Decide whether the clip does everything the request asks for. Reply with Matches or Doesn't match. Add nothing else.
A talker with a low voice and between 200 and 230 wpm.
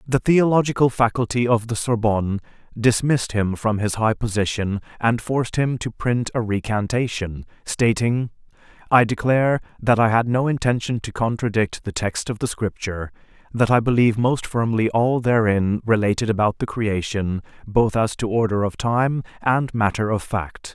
Doesn't match